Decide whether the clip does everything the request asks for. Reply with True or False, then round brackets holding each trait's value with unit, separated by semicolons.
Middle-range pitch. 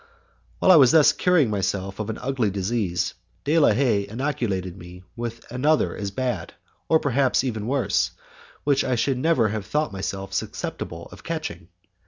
False (120 Hz)